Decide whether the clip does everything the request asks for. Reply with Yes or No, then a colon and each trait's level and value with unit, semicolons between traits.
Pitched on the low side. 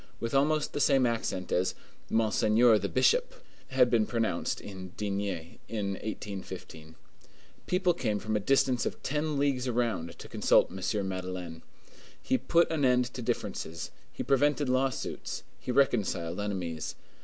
Yes: low, 115 Hz